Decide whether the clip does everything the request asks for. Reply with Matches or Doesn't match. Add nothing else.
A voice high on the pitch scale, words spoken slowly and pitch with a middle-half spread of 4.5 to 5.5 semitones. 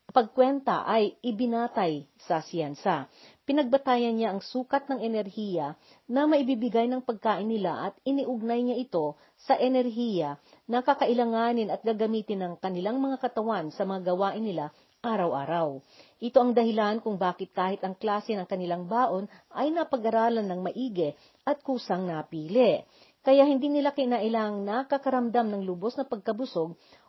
Doesn't match